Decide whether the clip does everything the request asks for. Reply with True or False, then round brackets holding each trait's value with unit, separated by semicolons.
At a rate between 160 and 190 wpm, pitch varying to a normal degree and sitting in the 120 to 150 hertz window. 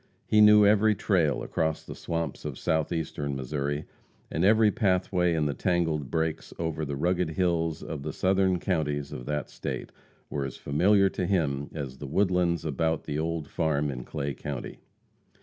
False (165 wpm; 3.9 semitones; 80 Hz)